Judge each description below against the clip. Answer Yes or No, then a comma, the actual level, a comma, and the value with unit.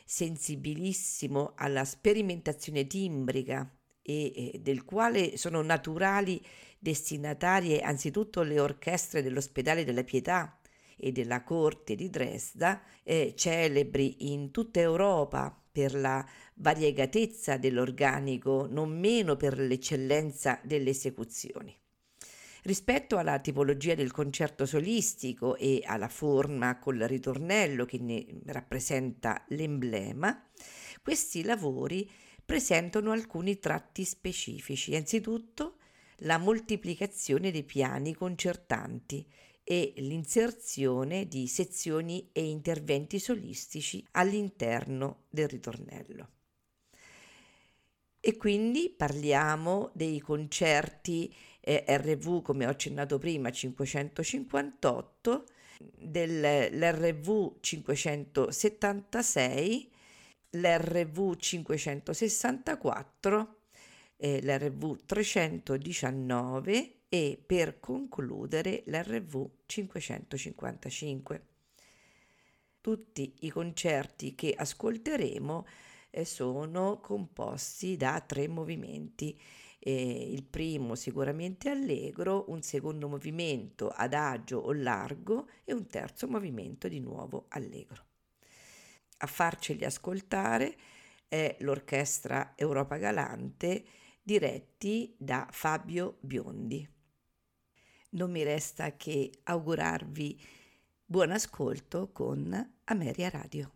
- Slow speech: Yes, slow, 85 wpm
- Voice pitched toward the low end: No, medium, 150 Hz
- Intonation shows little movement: No, average, 5.2 semitones